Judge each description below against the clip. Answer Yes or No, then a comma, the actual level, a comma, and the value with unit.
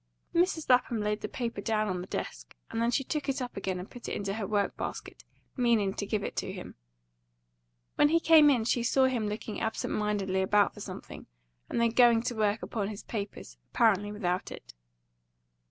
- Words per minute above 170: Yes, average, 200 wpm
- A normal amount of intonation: Yes, average, 3.1 semitones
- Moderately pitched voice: No, high, 220 Hz